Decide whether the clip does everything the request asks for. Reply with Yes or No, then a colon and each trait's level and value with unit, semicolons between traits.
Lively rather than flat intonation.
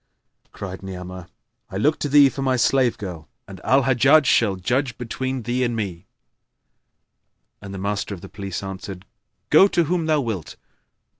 Yes: wide, 5.7 semitones